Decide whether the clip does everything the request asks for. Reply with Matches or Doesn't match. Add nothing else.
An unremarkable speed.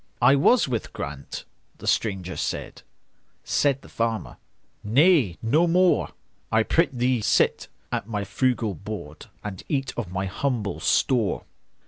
Doesn't match